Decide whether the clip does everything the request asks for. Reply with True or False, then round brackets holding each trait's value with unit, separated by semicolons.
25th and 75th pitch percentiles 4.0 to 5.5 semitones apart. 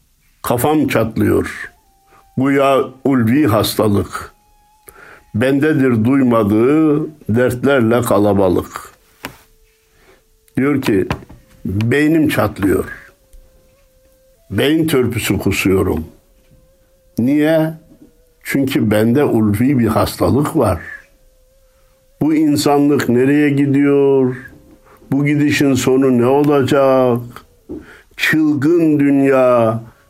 True (4.4 semitones)